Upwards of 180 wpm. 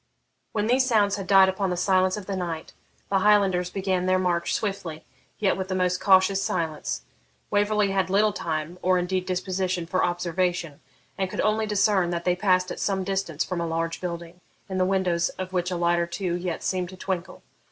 Yes: average, 200 wpm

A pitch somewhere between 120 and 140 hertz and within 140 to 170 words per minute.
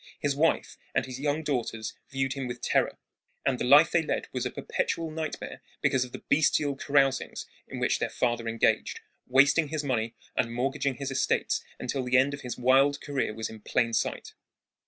No: low, 135 Hz; average, 190 wpm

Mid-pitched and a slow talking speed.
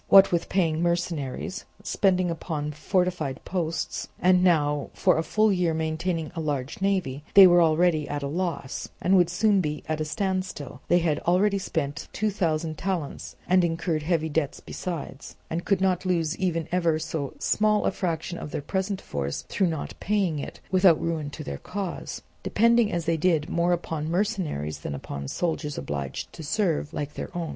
No: medium, 170 Hz; average, 180 wpm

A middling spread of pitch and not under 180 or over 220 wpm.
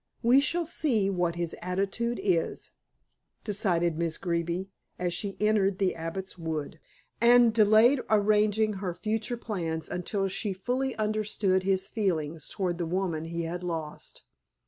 No: average, 4.0 semitones; average, 140 wpm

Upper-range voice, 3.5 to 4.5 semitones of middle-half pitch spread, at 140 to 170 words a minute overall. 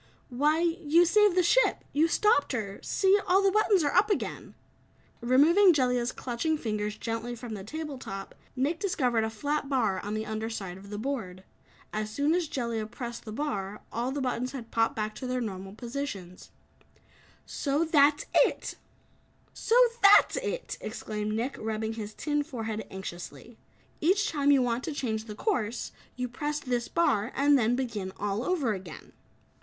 No: very high, 250 Hz; wide, 5.6 semitones; average, 165 wpm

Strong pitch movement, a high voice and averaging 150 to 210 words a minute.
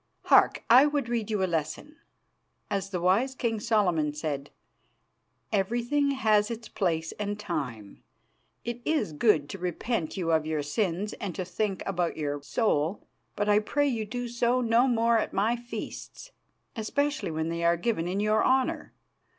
Yes: wide, 5.9 semitones; high, 210 Hz; average, 165 wpm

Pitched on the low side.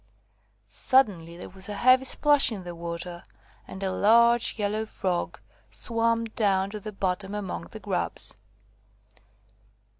No: high, 205 Hz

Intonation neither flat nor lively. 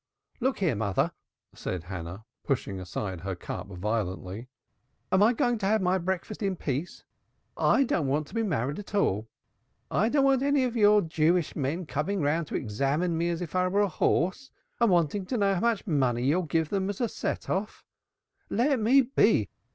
No: wide, 7.9 semitones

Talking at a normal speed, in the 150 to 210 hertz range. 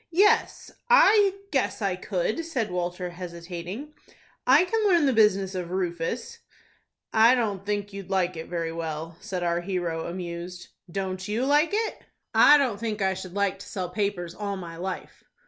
Yes: average, 165 wpm; high, 190 Hz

